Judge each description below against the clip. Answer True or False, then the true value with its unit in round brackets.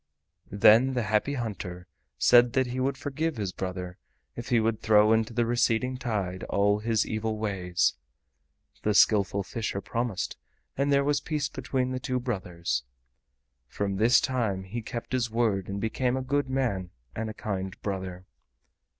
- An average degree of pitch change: True (4.4 semitones)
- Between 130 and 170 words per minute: True (160 wpm)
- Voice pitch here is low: True (110 Hz)